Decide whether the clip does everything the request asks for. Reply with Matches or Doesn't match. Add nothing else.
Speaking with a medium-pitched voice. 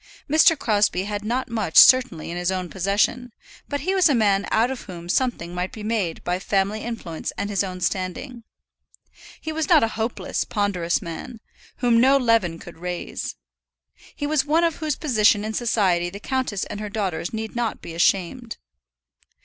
Doesn't match